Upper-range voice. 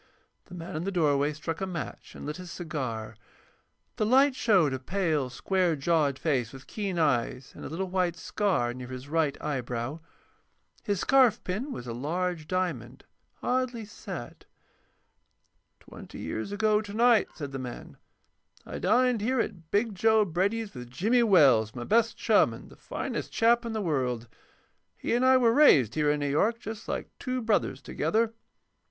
No: medium, 175 Hz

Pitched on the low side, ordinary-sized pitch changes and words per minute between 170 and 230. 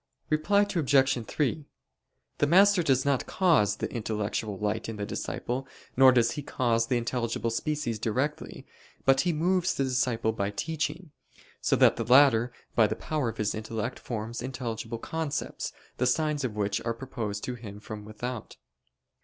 No: low, 125 Hz; average, 4.7 semitones; average, 160 wpm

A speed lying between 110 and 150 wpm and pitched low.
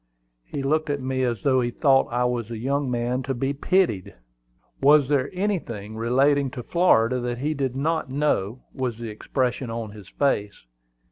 No: average, 180 wpm; low, 130 Hz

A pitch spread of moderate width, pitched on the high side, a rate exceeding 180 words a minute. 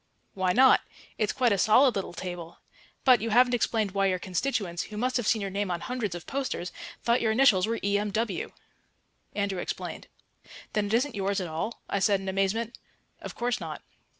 Yes: average, 3.7 semitones; high, 205 Hz; average, 190 wpm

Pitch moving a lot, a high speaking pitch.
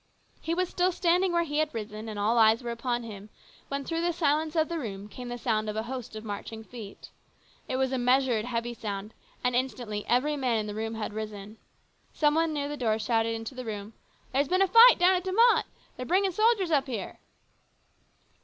Yes: wide, 6.3 semitones; very high, 250 Hz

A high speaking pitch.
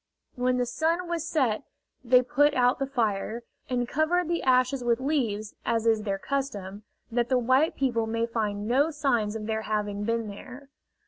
Yes: high, 245 Hz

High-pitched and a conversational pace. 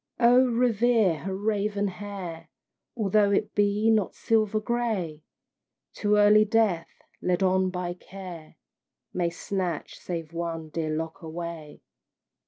No: high, 195 Hz; slow, 120 wpm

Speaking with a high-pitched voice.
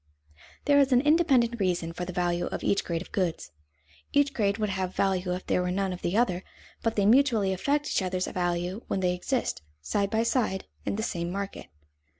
Yes: high, 195 Hz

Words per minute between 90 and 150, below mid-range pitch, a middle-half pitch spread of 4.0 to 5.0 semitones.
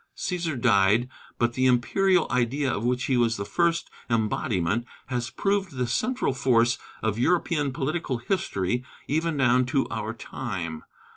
Yes: average, 145 wpm; low, 125 Hz; average, 4.5 semitones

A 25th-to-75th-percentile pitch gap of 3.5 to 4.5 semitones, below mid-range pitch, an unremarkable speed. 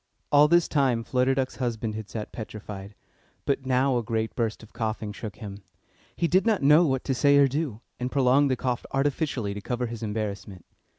Yes: average, 4.0 semitones; low, 125 Hz; average, 195 wpm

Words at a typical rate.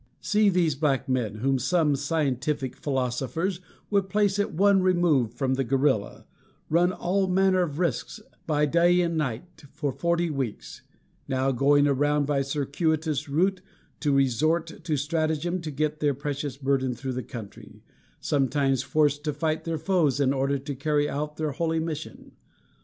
Yes: average, 160 wpm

